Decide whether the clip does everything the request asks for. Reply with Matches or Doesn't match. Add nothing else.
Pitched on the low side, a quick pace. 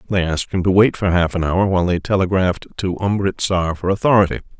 Matches